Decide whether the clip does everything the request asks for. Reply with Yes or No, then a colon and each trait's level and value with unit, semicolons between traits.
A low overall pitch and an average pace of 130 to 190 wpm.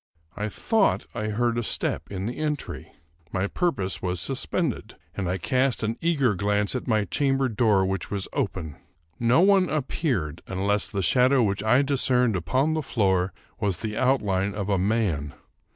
Yes: low, 110 Hz; average, 170 wpm